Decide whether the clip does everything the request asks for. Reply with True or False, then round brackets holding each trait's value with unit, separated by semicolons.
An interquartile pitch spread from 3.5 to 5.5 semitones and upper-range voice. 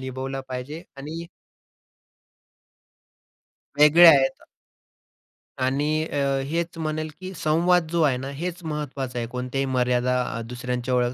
False (4.1 semitones; 140 Hz)